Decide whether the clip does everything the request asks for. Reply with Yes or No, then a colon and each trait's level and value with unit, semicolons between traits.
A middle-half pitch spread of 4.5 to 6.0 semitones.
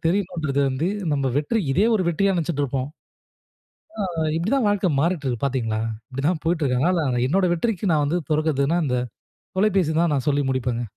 Yes: average, 4.9 semitones